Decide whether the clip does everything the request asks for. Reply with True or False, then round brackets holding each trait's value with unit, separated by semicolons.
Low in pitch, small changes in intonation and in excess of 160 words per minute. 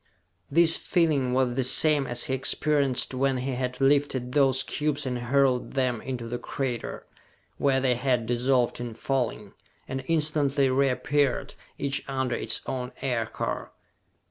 False (130 Hz; 2.0 semitones; 145 wpm)